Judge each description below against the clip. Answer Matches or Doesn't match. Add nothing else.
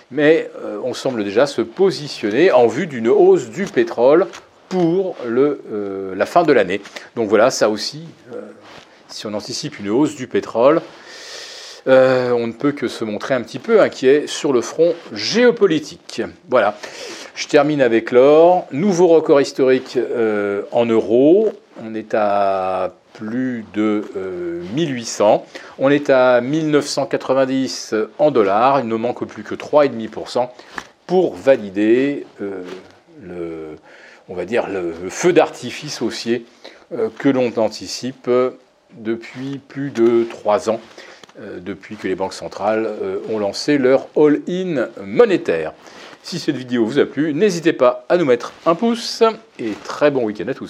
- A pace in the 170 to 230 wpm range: Doesn't match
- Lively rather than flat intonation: Matches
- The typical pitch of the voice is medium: Doesn't match